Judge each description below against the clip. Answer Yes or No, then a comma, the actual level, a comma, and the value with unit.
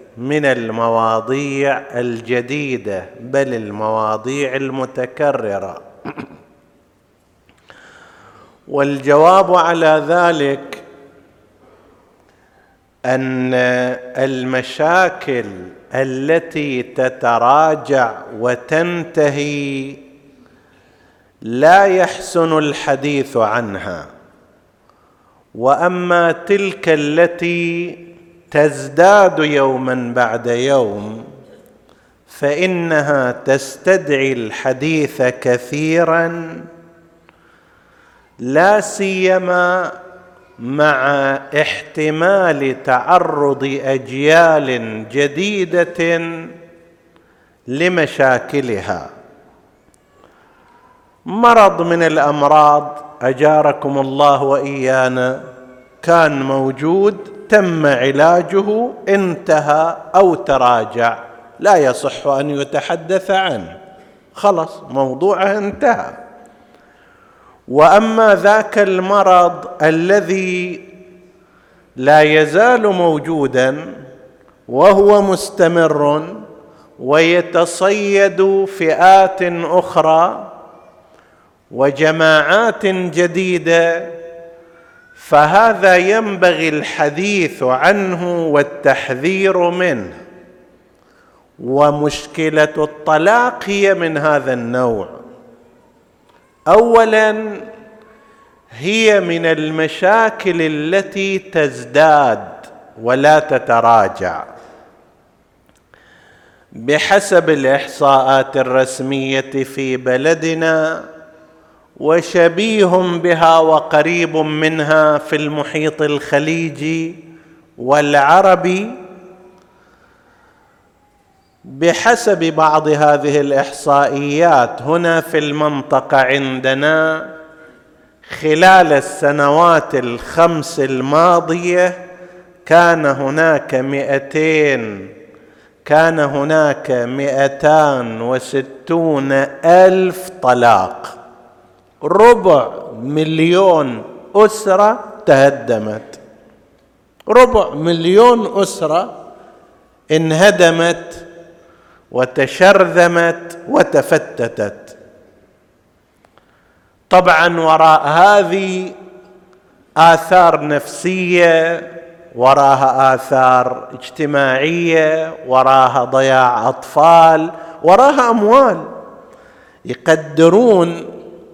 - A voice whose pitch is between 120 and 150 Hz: No, medium, 160 Hz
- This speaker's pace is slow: Yes, slow, 50 wpm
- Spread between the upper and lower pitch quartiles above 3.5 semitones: Yes, average, 4.6 semitones